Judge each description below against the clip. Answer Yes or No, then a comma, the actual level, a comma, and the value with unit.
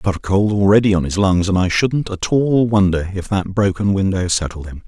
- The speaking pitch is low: Yes, very low, 95 Hz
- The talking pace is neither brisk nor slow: No, fast, 245 wpm